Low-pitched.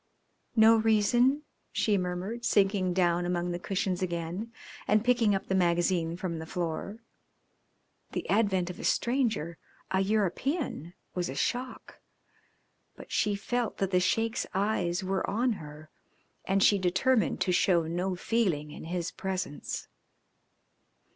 No: high, 190 Hz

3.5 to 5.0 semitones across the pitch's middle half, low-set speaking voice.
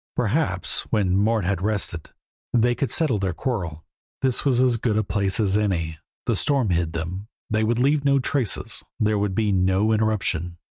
Yes: average, 4.2 semitones; low, 105 Hz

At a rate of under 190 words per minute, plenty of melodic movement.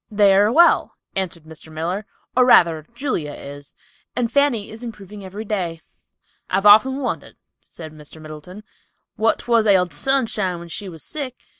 Yes: average, 155 wpm; wide, 5.7 semitones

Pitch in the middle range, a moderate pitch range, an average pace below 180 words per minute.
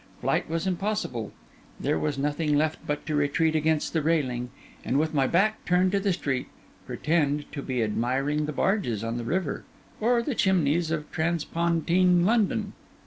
Yes: medium, 155 Hz; average, 4.0 semitones; average, 165 wpm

